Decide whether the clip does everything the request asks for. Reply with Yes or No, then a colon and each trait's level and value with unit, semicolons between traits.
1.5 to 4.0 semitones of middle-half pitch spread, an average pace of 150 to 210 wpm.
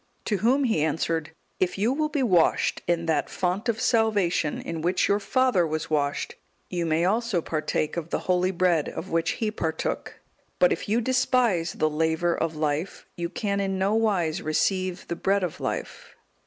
No: average, 4.8 semitones; average, 180 wpm